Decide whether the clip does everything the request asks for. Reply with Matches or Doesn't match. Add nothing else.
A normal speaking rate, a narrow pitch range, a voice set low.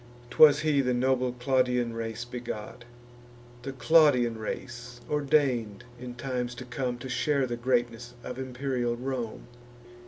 Doesn't match